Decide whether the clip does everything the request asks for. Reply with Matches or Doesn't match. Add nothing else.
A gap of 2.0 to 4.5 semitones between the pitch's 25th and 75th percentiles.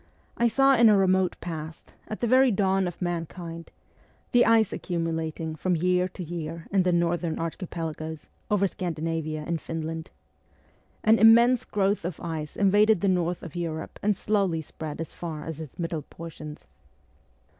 Matches